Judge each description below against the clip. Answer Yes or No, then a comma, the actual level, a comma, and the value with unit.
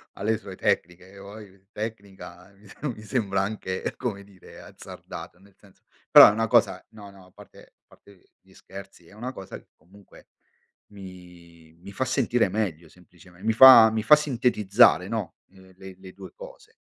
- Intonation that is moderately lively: Yes, average, 3.1 semitones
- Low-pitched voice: Yes, low, 100 Hz